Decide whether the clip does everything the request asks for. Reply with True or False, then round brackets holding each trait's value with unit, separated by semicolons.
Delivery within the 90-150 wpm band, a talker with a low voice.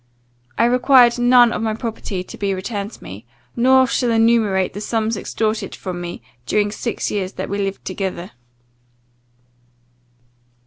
False (145 wpm; 215 Hz)